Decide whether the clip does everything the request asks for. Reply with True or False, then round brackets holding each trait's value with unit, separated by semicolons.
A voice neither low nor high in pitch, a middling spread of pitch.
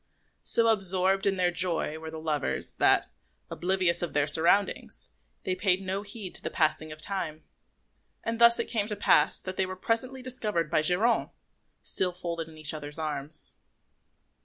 True (180 Hz; 4.2 semitones)